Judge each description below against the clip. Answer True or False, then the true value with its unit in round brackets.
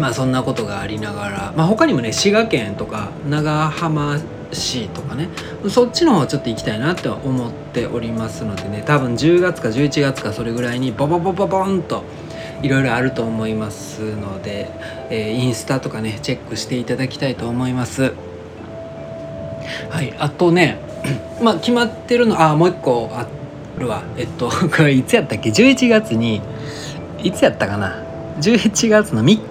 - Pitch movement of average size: False (6.7 semitones)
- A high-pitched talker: False (130 Hz)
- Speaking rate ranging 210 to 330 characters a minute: True (325 characters per minute)